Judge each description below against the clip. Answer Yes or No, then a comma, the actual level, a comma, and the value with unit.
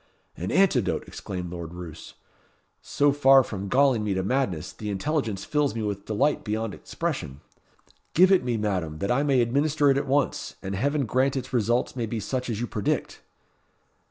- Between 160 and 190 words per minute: Yes, average, 180 wpm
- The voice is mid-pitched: No, low, 120 Hz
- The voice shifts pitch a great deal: Yes, wide, 5.7 semitones